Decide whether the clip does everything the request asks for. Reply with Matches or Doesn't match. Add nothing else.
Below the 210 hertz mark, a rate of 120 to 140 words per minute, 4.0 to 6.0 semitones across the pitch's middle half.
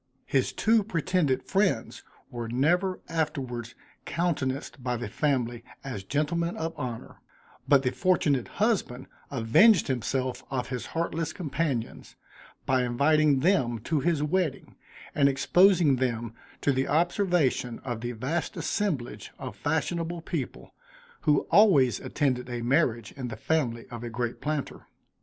Matches